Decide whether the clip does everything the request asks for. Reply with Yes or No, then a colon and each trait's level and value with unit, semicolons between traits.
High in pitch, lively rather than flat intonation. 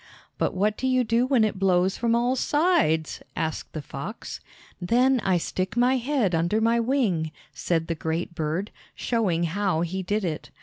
Yes: high, 195 Hz; wide, 6.1 semitones